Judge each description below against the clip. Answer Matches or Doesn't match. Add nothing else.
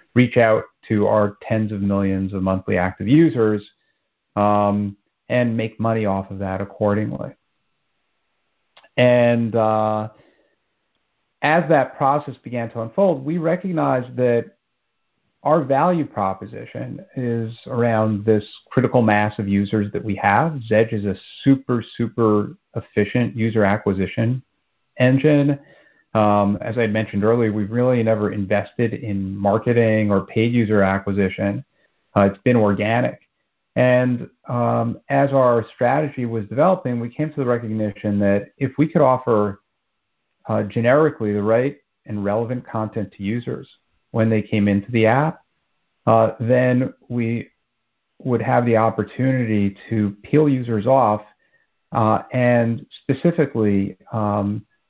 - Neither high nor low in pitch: Doesn't match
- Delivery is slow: Matches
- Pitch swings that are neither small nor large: Matches